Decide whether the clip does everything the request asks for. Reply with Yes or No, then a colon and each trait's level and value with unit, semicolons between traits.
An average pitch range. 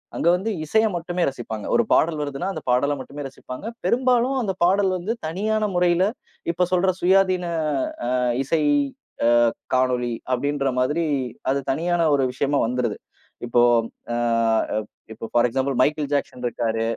No: wide, 6.0 semitones